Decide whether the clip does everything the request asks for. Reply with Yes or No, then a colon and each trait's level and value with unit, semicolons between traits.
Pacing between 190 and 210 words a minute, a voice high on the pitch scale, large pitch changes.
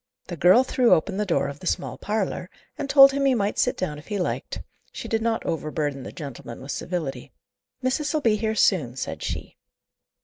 Yes: average, 200 wpm; high, 200 Hz; wide, 7.7 semitones